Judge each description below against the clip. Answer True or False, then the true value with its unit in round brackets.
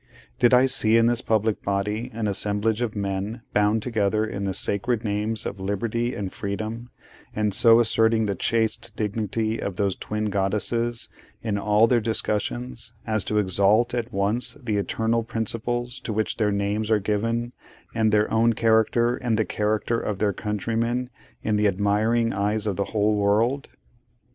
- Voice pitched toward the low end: True (110 Hz)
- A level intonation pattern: True (2.1 semitones)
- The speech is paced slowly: False (165 wpm)